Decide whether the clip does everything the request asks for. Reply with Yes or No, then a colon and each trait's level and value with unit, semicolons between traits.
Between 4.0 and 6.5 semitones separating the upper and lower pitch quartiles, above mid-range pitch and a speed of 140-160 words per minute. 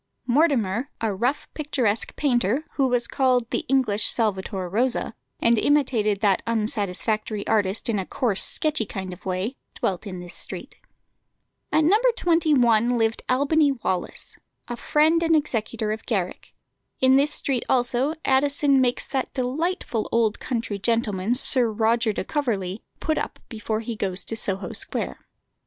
Yes: average, 4.4 semitones; high, 235 Hz; average, 145 wpm